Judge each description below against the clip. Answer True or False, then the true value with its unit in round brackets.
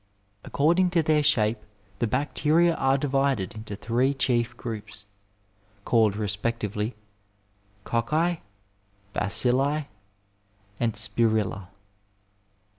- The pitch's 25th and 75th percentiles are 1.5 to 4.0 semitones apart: False (4.9 semitones)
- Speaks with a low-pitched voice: True (120 Hz)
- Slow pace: True (85 wpm)